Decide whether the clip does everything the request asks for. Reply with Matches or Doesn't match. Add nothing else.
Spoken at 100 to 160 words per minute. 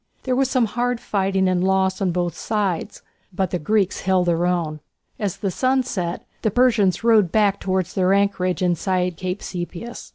Doesn't match